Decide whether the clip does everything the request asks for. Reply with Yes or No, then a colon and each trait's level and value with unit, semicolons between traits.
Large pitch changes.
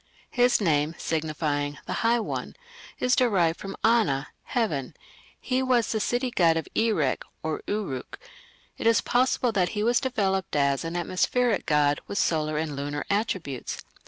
Yes: wide, 7.3 semitones